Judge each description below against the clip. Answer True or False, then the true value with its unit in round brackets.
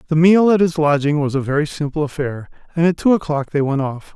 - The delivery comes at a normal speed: False (245 wpm)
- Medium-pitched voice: True (155 Hz)